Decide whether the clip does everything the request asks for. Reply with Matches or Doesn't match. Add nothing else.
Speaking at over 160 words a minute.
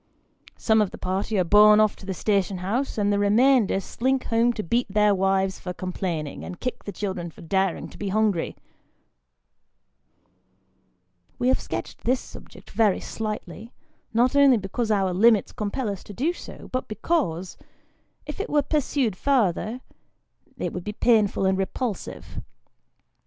Doesn't match